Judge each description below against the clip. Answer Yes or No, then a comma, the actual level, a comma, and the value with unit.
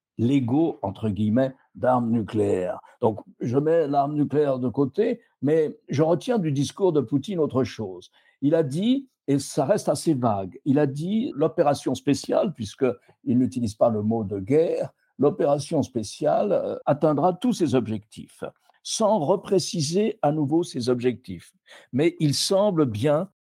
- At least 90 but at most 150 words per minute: Yes, slow, 145 wpm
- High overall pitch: No, medium, 145 Hz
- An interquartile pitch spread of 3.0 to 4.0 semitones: No, average, 5.2 semitones